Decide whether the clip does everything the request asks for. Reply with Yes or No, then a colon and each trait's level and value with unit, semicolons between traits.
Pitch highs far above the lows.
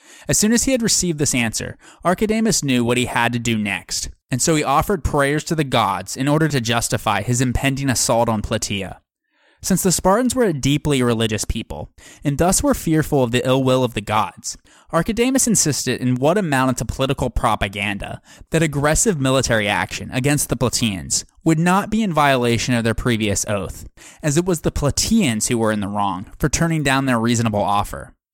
Yes: wide, 6.1 semitones